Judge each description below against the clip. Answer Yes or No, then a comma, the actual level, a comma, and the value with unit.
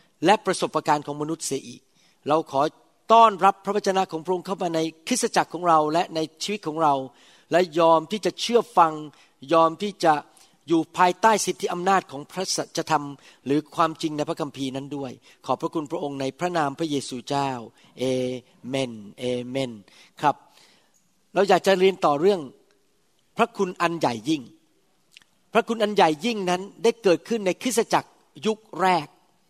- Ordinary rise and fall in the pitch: Yes, average, 4.7 semitones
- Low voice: No, medium, 165 Hz